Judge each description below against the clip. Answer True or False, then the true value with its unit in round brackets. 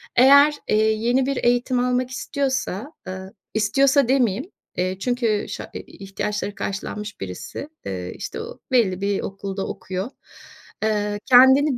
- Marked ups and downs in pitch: False (4.8 semitones)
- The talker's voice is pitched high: True (220 Hz)